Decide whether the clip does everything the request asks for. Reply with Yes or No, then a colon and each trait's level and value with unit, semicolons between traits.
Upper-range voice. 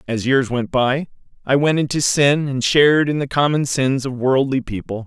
No: low, 135 Hz